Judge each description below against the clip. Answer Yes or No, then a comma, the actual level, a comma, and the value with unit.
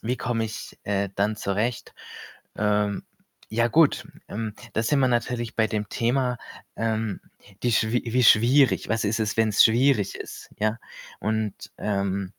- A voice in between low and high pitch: No, low, 110 Hz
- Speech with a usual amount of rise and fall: No, narrow, 2.3 semitones